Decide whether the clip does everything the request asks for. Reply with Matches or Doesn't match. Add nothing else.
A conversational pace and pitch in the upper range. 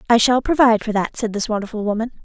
Doesn't match